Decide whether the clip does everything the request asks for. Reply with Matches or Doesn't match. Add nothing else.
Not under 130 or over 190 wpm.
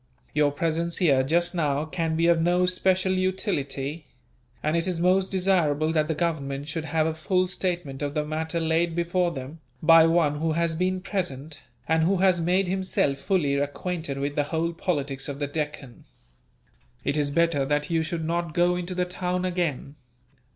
Matches